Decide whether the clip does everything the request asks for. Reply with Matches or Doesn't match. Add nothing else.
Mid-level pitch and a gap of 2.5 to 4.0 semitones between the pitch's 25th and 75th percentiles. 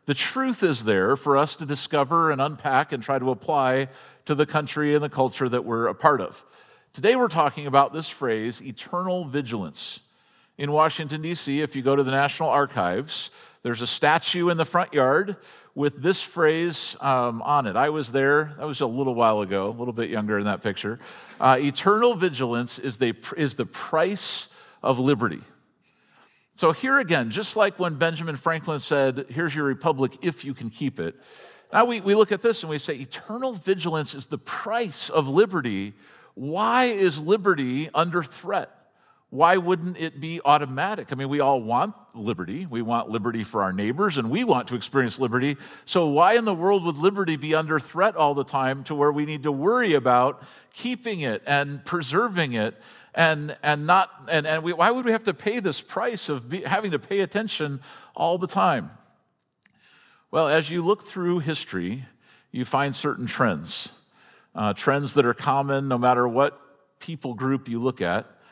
Doesn't match